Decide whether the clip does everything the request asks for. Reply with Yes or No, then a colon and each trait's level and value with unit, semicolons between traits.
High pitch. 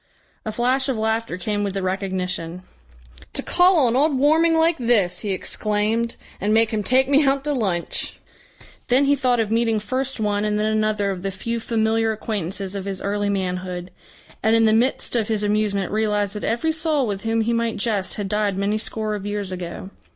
Yes: high, 215 Hz